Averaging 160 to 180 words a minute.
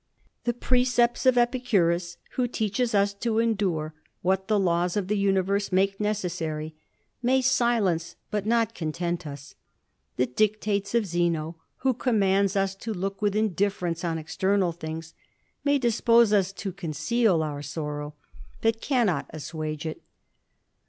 No: average, 145 wpm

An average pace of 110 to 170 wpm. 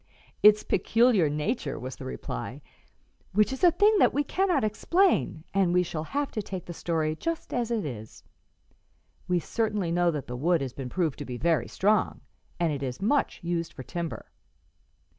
No: average, 180 wpm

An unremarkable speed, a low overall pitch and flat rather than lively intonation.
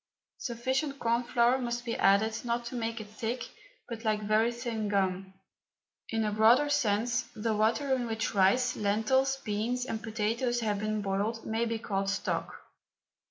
No: average, 160 wpm; high, 225 Hz; narrow, 2.1 semitones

